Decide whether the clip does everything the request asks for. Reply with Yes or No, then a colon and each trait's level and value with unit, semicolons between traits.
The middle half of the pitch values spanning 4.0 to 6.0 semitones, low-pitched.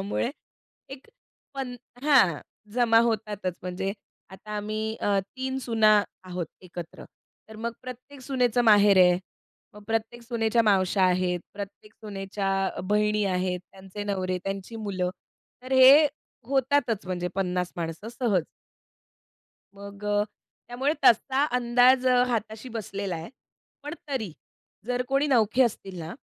No: average, 4.4 semitones; high, 215 Hz